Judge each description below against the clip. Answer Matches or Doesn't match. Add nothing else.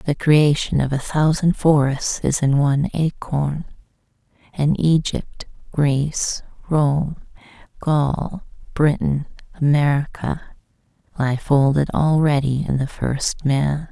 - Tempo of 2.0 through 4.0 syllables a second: Matches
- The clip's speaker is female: Matches